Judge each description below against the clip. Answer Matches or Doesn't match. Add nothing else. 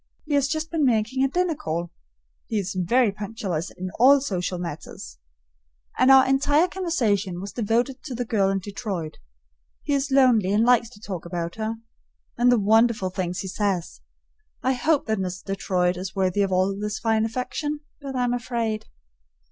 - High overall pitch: Matches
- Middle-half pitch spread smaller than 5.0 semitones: Doesn't match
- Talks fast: Doesn't match